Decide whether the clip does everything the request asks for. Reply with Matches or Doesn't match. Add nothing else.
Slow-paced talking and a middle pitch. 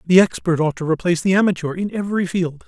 Doesn't match